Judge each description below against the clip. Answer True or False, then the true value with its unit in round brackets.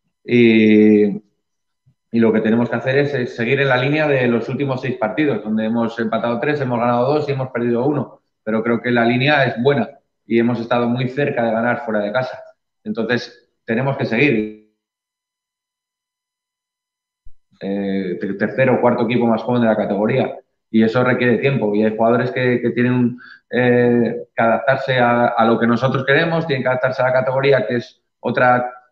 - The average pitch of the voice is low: True (120 Hz)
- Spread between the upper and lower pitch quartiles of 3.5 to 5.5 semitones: False (3.1 semitones)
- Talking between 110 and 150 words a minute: False (185 wpm)